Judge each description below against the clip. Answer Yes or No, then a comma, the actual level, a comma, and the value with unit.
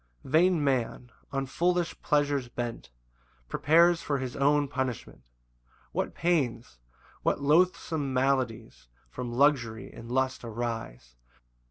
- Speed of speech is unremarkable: No, slow, 115 wpm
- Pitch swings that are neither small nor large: Yes, average, 3.8 semitones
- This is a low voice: Yes, low, 130 Hz